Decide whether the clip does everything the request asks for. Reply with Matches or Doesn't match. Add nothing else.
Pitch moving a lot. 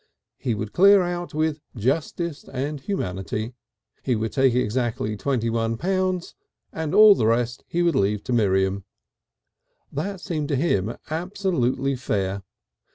Matches